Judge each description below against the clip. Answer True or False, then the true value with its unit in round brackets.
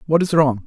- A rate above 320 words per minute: False (270 wpm)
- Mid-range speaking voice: True (145 Hz)